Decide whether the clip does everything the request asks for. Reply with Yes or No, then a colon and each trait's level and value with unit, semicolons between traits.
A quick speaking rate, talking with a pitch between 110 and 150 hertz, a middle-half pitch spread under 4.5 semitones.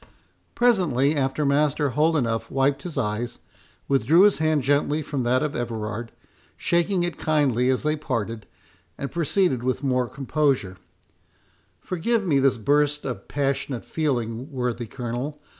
No: slow, 135 wpm; medium, 140 Hz; average, 3.8 semitones